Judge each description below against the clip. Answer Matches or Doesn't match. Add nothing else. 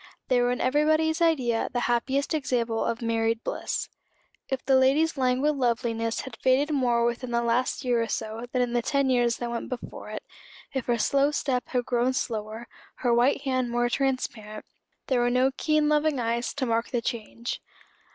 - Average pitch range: Doesn't match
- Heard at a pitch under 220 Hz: Doesn't match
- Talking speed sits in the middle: Matches